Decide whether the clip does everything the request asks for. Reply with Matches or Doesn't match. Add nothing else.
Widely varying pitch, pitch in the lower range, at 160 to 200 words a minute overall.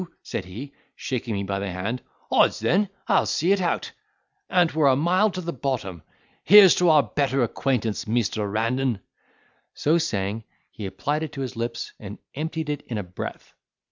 Matches